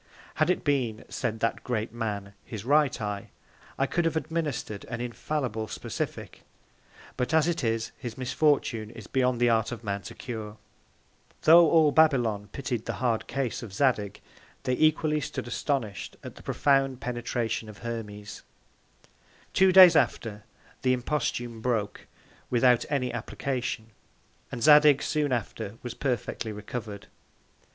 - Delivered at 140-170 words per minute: Yes, average, 145 wpm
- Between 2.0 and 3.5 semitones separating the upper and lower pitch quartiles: No, average, 4.2 semitones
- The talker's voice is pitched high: No, low, 120 Hz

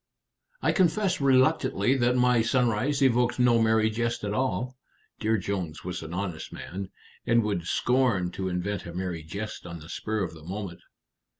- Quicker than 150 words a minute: Yes, average, 170 wpm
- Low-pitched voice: Yes, low, 110 Hz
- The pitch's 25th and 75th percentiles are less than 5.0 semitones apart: No, wide, 5.4 semitones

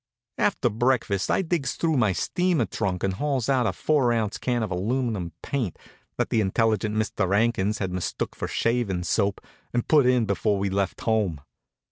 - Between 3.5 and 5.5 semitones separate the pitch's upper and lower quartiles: Yes, average, 4.3 semitones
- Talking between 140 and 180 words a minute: Yes, average, 175 wpm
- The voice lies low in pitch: Yes, low, 110 Hz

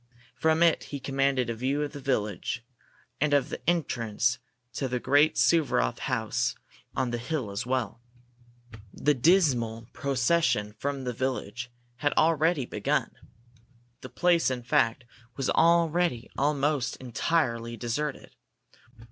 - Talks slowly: Yes, slow, 130 wpm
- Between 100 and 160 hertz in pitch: Yes, low, 135 Hz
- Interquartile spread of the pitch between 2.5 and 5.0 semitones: Yes, average, 4.1 semitones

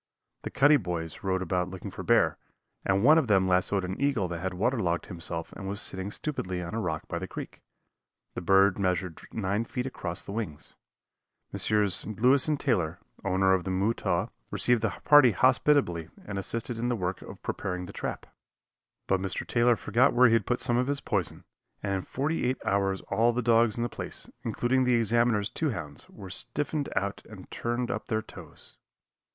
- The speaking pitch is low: Yes, low, 100 Hz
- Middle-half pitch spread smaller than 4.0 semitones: No, average, 4.5 semitones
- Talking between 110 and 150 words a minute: No, average, 190 wpm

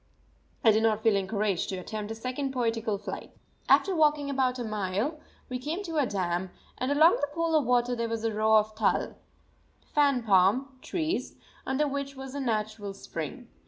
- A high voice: Yes, high, 240 Hz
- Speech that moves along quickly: No, average, 185 wpm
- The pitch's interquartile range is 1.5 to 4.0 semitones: No, average, 4.7 semitones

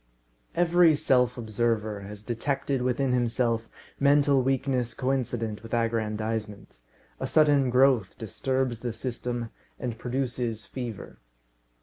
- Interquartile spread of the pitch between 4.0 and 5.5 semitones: No, average, 2.9 semitones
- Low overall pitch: Yes, low, 120 Hz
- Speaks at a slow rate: Yes, slow, 105 wpm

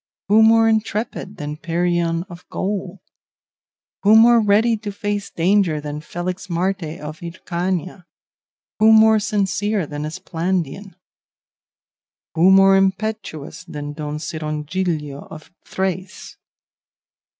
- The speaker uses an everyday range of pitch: Yes, average, 4.1 semitones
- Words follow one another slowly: Yes, slow, 105 wpm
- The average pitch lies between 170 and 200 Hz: Yes, medium, 185 Hz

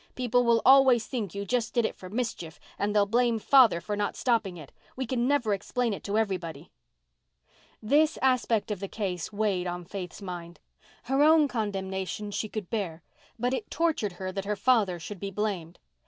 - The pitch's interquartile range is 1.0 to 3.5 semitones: No, average, 4.4 semitones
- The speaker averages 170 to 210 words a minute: Yes, average, 185 wpm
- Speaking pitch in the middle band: No, high, 210 Hz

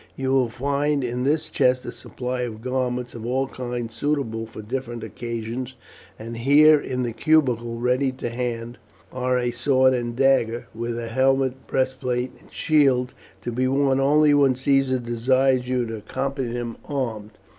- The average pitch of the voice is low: Yes, low, 125 Hz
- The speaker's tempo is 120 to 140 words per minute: No, average, 165 wpm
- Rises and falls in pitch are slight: Yes, narrow, 2.1 semitones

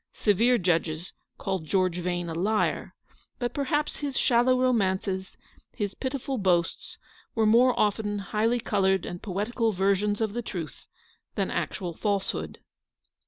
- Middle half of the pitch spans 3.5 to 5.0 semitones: Yes, average, 4.3 semitones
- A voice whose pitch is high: Yes, high, 205 Hz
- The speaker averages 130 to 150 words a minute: Yes, slow, 135 wpm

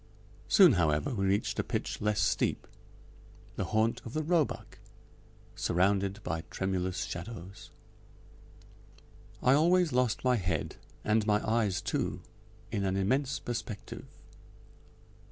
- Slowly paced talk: Yes, slow, 120 wpm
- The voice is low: Yes, low, 105 Hz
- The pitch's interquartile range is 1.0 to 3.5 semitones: No, average, 4.8 semitones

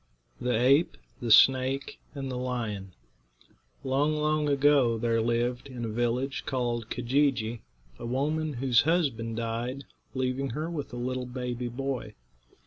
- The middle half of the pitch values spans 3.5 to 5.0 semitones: No, narrow, 2.6 semitones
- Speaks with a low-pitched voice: Yes, low, 125 Hz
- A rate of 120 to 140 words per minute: Yes, slow, 135 wpm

